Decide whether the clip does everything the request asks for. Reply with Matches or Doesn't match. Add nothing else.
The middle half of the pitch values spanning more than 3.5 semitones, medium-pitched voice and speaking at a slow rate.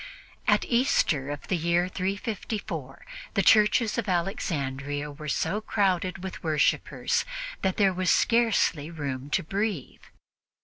Matches